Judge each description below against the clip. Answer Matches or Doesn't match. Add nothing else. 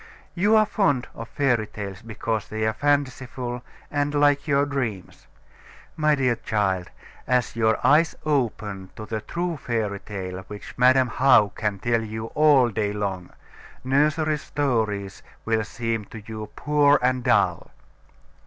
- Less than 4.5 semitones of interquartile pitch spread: Doesn't match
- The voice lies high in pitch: Doesn't match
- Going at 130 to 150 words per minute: Matches